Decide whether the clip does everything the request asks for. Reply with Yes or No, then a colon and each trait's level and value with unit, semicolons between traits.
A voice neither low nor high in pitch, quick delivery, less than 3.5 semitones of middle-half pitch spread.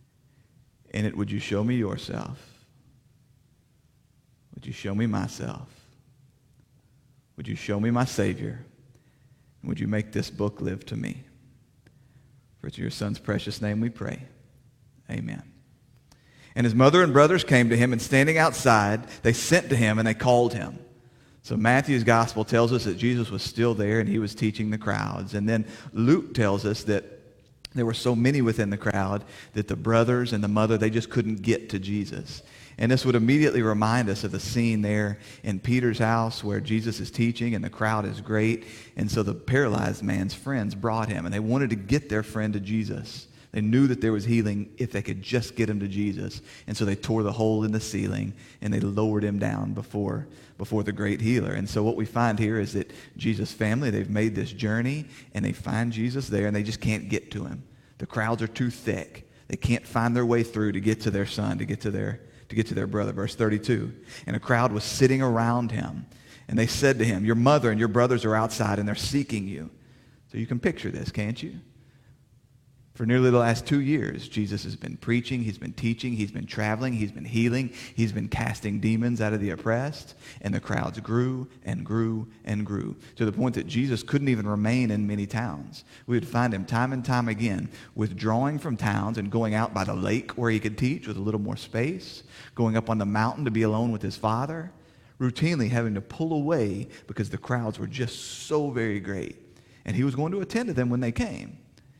No: low, 115 Hz; fast, 210 wpm; average, 3.1 semitones